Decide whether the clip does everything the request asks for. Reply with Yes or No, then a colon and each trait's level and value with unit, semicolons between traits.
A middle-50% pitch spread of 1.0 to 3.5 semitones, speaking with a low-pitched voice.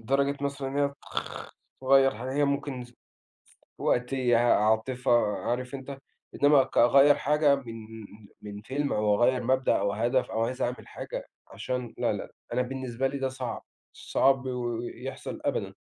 Yes: narrow, 2.4 semitones; low, 130 Hz